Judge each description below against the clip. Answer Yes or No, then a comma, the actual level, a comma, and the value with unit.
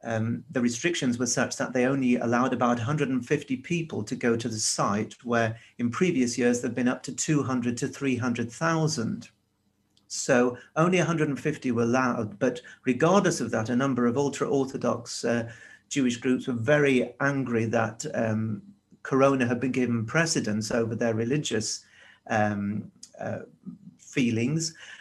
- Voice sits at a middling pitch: No, low, 125 Hz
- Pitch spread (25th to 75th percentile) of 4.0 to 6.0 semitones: No, average, 3.4 semitones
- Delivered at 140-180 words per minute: Yes, average, 145 wpm